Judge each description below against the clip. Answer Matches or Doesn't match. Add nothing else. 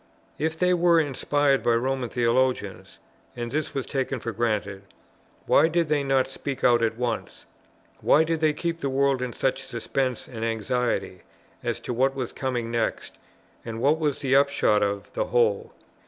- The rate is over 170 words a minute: Matches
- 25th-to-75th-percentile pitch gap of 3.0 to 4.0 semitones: Matches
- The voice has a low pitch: Matches